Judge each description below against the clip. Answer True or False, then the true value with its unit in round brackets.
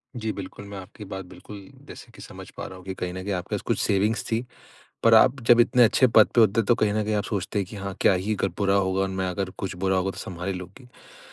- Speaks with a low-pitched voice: True (100 Hz)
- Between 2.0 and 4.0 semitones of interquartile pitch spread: True (2.6 semitones)